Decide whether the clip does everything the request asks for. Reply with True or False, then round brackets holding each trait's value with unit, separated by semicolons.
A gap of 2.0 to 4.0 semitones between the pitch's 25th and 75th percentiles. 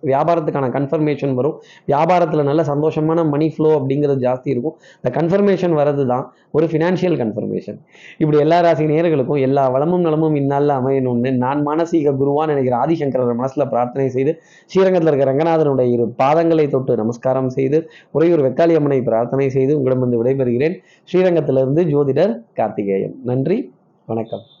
True (3.6 semitones)